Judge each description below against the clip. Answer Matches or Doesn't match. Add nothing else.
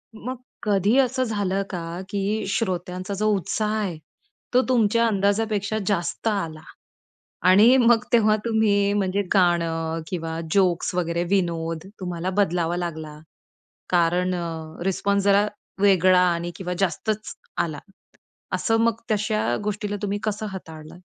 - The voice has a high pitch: Matches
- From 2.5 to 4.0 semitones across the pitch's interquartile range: Matches